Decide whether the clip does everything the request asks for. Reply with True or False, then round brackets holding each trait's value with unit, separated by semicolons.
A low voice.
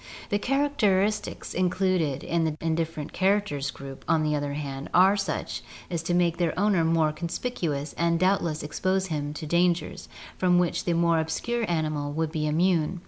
False (170 Hz)